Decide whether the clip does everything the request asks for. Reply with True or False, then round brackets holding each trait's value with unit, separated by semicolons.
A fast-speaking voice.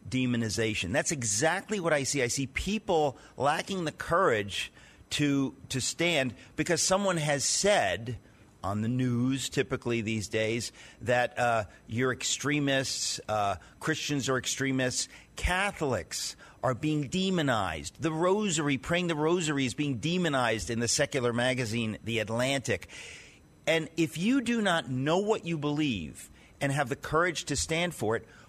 False (145 wpm)